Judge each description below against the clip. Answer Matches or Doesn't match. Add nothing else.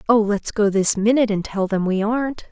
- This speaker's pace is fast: Matches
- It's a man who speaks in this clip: Doesn't match